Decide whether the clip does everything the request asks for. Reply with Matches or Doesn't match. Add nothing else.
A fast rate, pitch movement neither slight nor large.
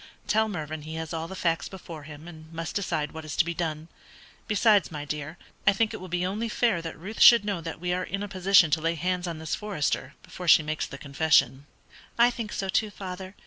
Matches